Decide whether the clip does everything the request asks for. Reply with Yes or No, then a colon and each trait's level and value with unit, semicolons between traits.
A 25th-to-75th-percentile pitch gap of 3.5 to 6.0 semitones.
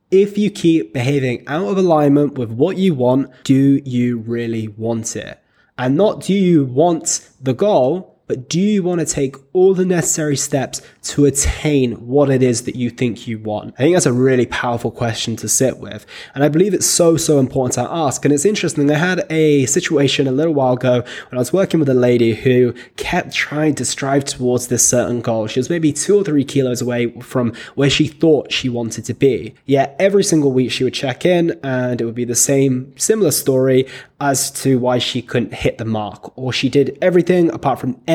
Yes: average, 3.9 semitones